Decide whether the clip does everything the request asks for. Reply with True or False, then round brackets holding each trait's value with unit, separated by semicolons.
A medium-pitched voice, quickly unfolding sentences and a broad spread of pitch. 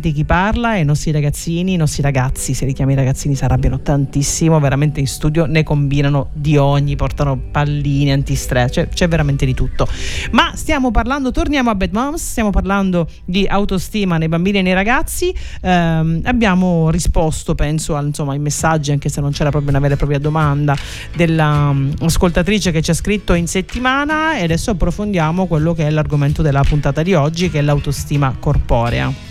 False (155 Hz; 175 wpm; 4.4 semitones)